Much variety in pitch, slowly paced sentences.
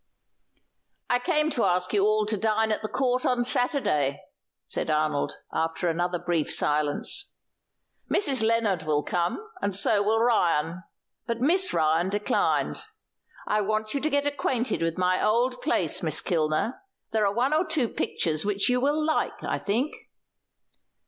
No: wide, 6.3 semitones; average, 155 wpm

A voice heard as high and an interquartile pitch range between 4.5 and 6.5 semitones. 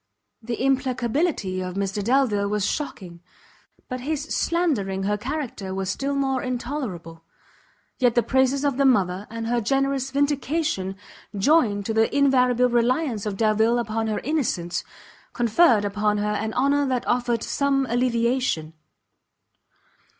Yes: high, 240 Hz; average, 4.8 semitones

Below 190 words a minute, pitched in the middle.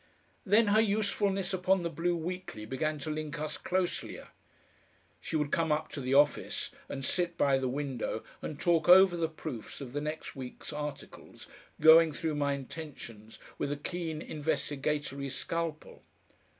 Yes: average, 155 wpm; medium, 155 Hz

